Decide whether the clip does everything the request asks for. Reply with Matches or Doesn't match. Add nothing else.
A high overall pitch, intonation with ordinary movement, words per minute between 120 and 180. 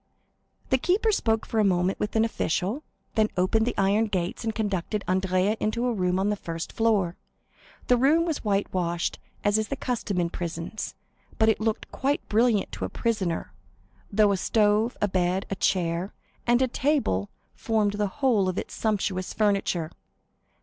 Matches